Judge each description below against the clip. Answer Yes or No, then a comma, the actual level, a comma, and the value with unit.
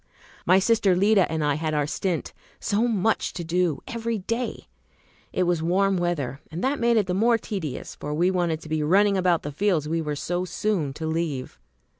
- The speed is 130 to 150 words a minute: No, average, 200 wpm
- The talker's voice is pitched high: No, medium, 180 Hz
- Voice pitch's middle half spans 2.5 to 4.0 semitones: No, average, 4.4 semitones